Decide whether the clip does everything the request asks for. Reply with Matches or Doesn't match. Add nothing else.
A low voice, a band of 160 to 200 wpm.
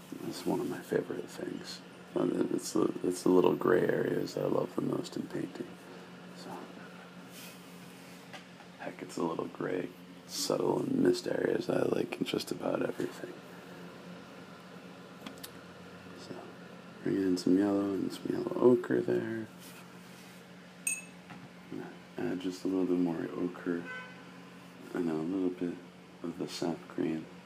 Doesn't match